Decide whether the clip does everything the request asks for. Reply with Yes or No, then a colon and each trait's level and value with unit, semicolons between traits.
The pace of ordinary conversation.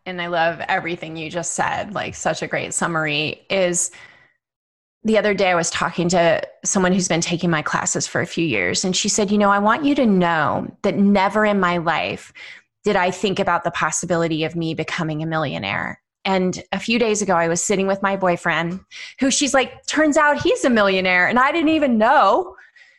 No: fast, 210 wpm